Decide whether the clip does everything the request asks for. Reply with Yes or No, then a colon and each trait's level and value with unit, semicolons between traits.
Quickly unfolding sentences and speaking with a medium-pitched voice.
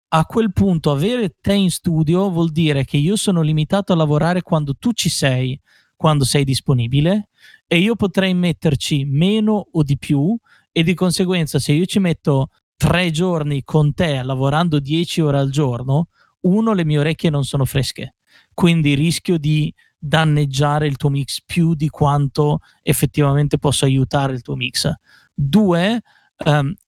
No: average, 160 wpm; medium, 155 Hz